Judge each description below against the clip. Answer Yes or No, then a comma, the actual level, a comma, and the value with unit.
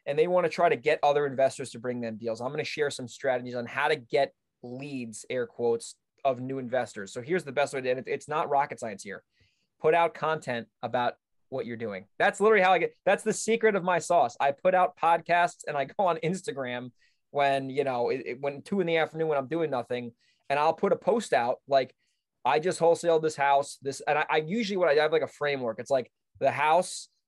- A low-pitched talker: No, medium, 145 Hz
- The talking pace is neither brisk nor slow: No, fast, 240 wpm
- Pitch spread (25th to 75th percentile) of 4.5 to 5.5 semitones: Yes, average, 5.2 semitones